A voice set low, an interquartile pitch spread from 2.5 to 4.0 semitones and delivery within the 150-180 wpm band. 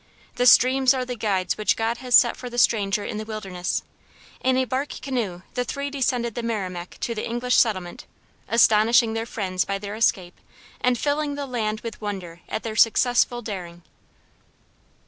No: high, 225 Hz; average, 3.6 semitones; average, 175 wpm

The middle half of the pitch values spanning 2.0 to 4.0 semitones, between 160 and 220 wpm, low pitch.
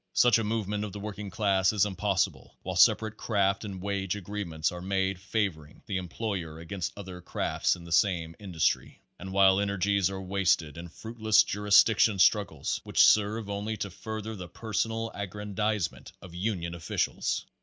Yes: narrow, 2.5 semitones; average, 165 wpm; low, 100 Hz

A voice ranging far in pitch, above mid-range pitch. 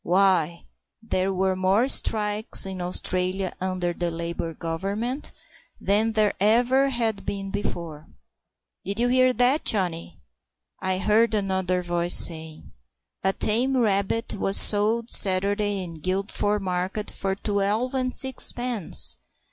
No: average, 3.3 semitones; high, 195 Hz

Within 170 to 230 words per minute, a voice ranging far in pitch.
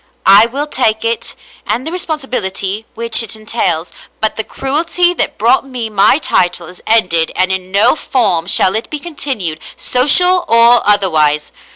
No: average, 160 wpm; wide, 5.9 semitones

